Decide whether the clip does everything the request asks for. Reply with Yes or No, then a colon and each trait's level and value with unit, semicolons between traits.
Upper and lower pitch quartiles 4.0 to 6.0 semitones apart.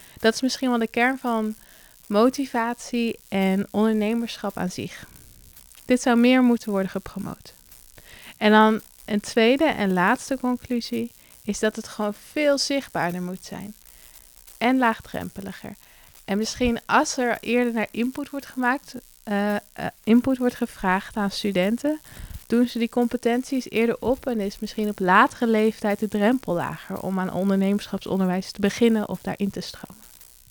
No: average, 3.3 semitones